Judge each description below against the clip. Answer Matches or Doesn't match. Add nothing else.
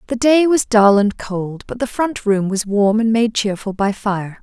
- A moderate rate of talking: Doesn't match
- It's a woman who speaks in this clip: Matches